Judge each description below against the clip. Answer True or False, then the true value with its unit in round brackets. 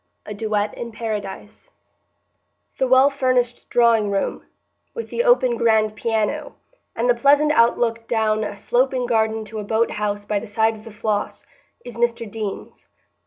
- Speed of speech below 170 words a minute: True (160 wpm)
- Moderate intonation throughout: False (2.3 semitones)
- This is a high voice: True (225 Hz)